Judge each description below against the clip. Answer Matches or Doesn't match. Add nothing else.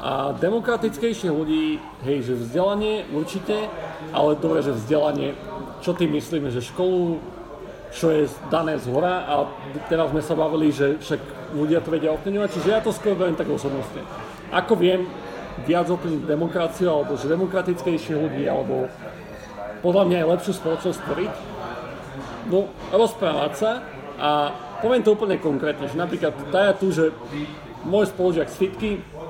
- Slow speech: Doesn't match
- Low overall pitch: Doesn't match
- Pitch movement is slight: Doesn't match